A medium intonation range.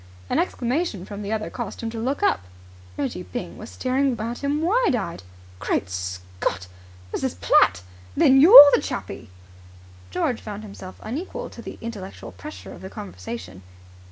No: wide, 8.1 semitones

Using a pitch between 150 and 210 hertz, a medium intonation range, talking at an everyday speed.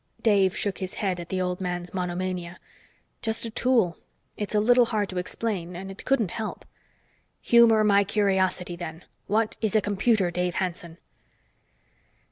Yes: high, 190 Hz; average, 3.2 semitones; average, 155 wpm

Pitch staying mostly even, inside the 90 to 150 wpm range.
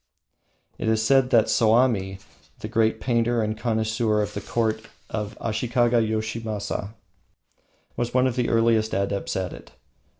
Yes: narrow, 1.6 semitones; average, 140 wpm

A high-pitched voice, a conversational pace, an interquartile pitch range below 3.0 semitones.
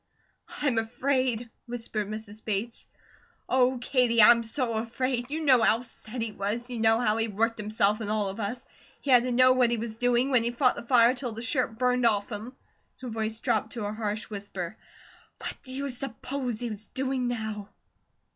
Yes: high, 235 Hz; average, 195 wpm; narrow, 2.4 semitones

